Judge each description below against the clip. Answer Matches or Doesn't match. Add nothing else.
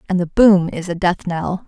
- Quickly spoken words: Matches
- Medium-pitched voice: Matches